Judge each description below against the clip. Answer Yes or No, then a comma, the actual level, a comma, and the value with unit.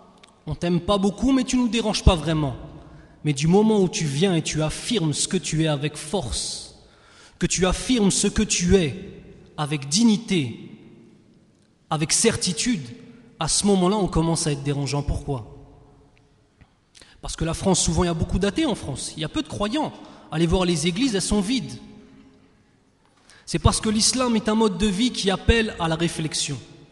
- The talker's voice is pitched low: No, medium, 180 Hz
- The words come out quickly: No, average, 190 wpm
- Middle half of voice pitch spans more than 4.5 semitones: Yes, wide, 5.4 semitones